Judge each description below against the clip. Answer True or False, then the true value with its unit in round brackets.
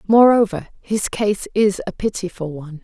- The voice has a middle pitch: False (200 Hz)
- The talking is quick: False (150 wpm)